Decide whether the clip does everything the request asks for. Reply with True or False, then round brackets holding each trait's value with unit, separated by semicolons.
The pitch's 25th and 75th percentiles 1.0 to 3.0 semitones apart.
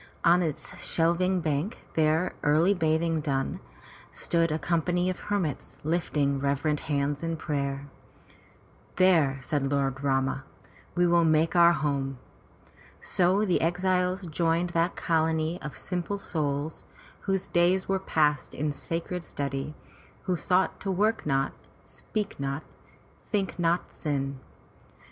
False (3.6 semitones)